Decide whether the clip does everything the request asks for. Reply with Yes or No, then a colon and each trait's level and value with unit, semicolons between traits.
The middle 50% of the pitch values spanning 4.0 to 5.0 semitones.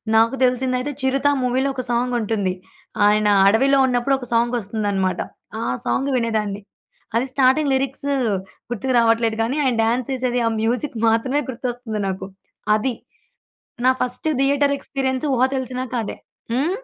No: average, 2.9 semitones